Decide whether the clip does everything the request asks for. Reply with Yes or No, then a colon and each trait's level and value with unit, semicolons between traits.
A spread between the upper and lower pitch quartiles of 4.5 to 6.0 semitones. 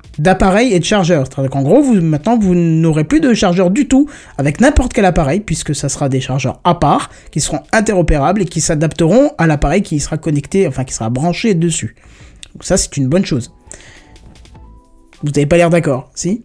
Yes: average, 5.1 semitones